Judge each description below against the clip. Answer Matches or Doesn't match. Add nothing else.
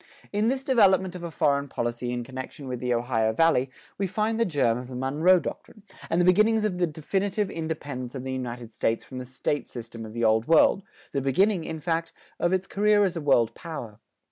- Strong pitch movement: Matches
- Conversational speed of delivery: Doesn't match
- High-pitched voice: Doesn't match